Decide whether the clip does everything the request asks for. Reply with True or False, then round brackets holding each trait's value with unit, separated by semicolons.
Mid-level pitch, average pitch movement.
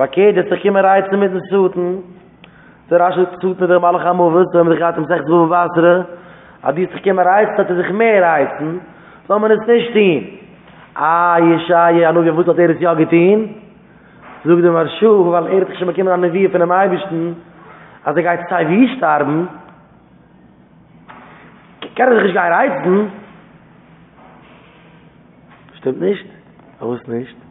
False (175 Hz; 2.2 semitones)